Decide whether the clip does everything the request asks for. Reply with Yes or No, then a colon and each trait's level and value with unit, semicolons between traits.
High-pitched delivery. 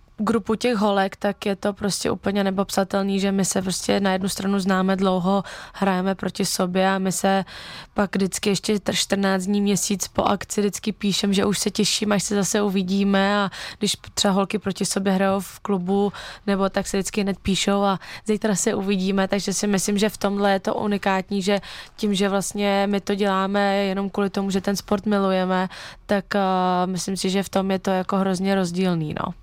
Yes: high, 195 Hz